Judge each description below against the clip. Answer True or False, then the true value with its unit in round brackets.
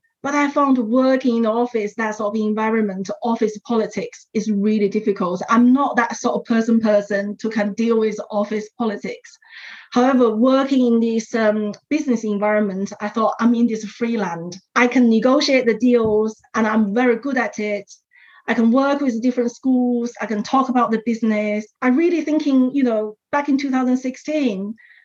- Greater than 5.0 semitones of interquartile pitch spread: False (3.2 semitones)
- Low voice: False (230 Hz)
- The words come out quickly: False (180 wpm)